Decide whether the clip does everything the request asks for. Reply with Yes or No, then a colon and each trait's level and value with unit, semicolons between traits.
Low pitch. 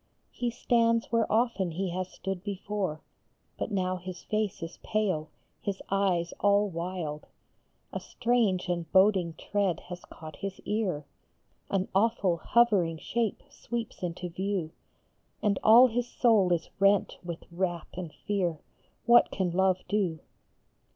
No: high, 190 Hz